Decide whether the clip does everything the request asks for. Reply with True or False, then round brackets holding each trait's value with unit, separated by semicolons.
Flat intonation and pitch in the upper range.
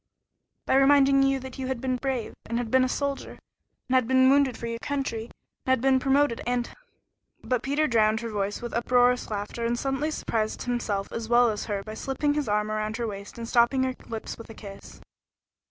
False (3.1 semitones; 245 Hz)